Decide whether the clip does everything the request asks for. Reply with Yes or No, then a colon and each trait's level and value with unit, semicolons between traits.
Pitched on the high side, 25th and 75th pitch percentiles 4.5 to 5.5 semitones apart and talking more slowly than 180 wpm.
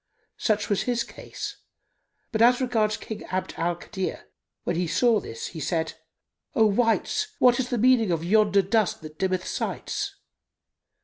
Yes: high, 210 Hz; average, 4.9 semitones; average, 160 wpm